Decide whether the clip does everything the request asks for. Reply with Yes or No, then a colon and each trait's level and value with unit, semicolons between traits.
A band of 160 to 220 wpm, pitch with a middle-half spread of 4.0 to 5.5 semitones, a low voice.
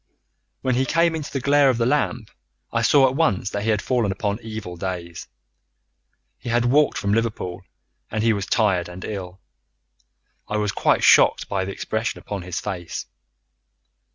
Yes: average, 180 wpm; average, 4.5 semitones; low, 110 Hz